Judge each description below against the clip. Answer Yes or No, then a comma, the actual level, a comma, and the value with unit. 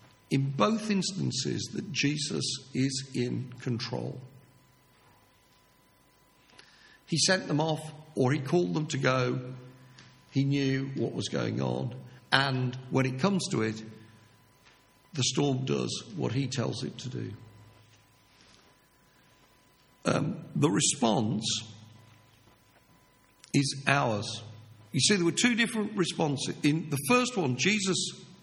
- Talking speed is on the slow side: Yes, slow, 120 wpm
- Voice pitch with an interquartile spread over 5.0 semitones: Yes, wide, 5.5 semitones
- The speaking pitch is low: Yes, low, 130 Hz